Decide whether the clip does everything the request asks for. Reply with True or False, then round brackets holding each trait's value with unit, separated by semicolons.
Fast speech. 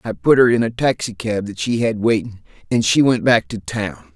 True (230 wpm)